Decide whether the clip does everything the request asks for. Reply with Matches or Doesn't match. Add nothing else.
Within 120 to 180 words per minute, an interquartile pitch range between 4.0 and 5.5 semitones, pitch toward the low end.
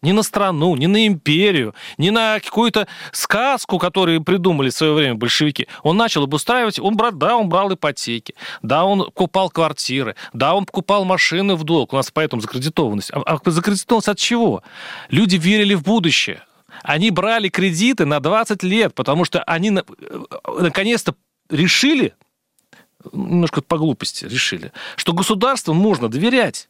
Doesn't match